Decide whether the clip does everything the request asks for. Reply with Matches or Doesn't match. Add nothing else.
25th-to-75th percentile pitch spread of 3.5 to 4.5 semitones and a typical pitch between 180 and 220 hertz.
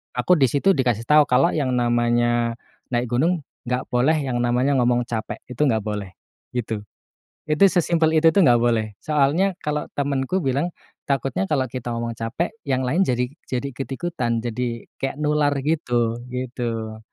Doesn't match